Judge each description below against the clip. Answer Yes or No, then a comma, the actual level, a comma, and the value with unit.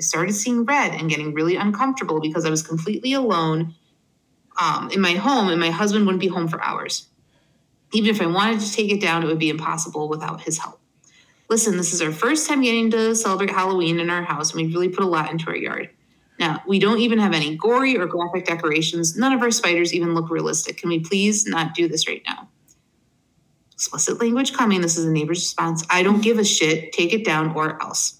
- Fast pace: Yes, fast, 225 wpm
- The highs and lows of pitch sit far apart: No, average, 4.6 semitones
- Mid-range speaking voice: Yes, medium, 175 Hz